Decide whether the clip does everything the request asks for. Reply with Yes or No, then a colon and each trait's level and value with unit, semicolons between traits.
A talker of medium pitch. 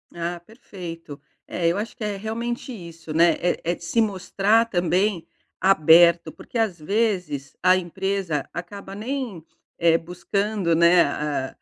Yes: medium, 180 Hz